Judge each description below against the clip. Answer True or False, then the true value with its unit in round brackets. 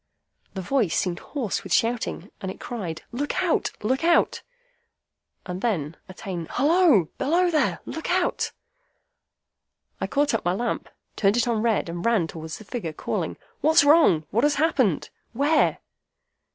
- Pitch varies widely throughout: True (8.0 semitones)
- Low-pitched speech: False (235 Hz)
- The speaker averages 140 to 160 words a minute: True (150 wpm)